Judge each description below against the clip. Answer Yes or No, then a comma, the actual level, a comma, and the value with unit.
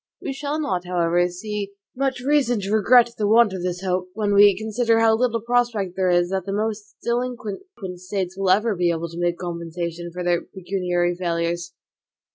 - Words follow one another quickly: No, average, 185 wpm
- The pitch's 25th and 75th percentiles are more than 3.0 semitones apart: Yes, average, 4.3 semitones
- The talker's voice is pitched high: Yes, high, 195 Hz